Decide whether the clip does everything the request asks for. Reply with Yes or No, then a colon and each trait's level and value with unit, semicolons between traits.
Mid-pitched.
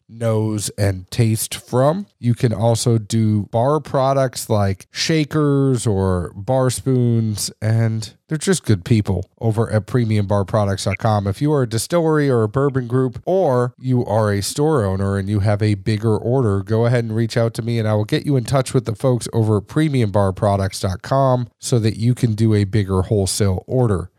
No: low, 115 Hz